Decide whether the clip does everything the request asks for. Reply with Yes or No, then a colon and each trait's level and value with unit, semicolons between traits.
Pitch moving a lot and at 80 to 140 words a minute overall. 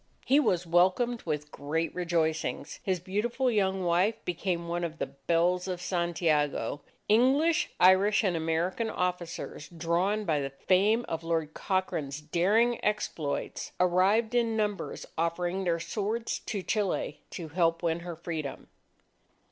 No: average, 3.8 semitones; slow, 135 wpm